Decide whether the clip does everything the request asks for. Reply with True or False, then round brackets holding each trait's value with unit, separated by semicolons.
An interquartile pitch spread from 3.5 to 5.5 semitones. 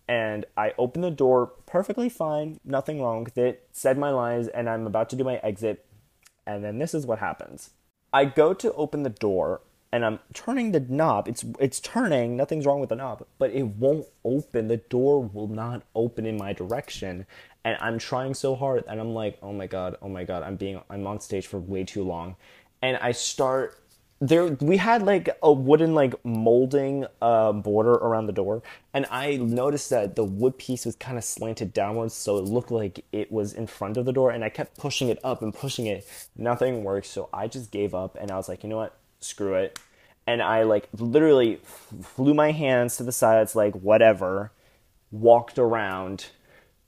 True (4.2 semitones)